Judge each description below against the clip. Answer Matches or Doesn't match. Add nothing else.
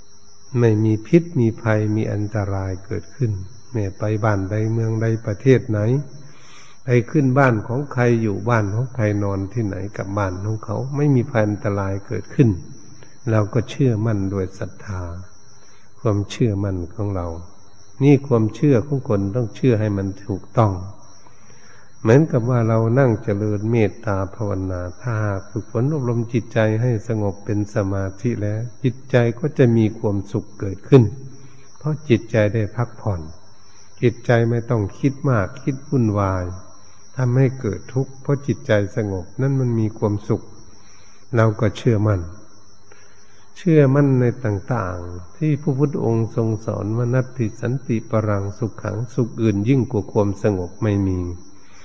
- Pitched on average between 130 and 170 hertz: Doesn't match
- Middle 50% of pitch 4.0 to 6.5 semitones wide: Doesn't match